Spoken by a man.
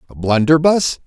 Yes: male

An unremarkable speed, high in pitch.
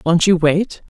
No: average, 180 wpm; medium, 175 Hz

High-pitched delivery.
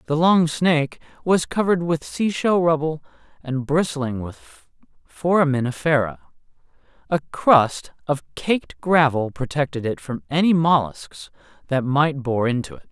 No: medium, 145 Hz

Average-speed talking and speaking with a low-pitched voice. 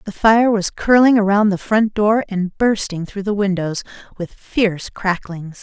No: average, 170 wpm; high, 200 Hz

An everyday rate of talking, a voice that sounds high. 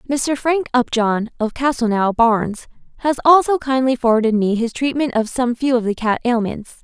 Yes: average, 175 wpm; high, 245 Hz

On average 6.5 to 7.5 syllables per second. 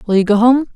Yes: 6.7 syllables/s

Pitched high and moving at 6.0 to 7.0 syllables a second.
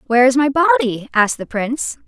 Yes: very high, 255 Hz; 6.1 syllables/s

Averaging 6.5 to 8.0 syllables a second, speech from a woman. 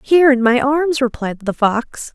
No: 4.4 syllables/s; female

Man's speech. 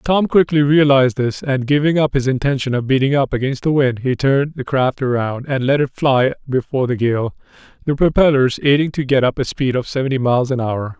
Yes: male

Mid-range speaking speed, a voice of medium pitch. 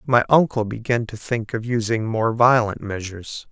No: average, 170 wpm; low, 115 Hz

